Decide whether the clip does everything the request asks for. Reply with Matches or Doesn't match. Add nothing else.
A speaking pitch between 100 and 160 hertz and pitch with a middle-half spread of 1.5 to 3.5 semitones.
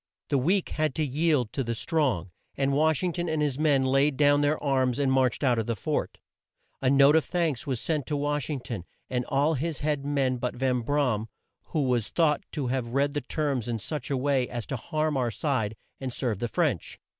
Matches